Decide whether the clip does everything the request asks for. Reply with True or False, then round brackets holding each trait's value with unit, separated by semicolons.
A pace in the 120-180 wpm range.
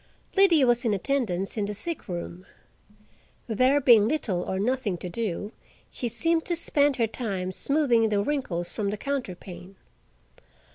True (150 wpm)